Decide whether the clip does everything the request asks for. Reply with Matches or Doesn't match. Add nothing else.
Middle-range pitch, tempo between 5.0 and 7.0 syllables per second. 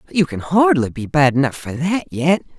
Matches